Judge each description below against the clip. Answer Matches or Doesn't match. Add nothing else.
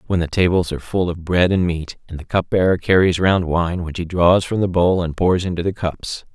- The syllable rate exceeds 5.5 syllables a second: Doesn't match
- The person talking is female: Doesn't match